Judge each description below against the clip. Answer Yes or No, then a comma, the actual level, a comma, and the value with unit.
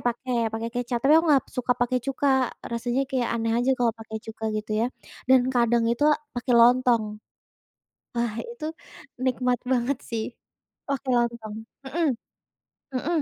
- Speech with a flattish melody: Yes, narrow, 1.9 semitones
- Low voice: No, high, 245 Hz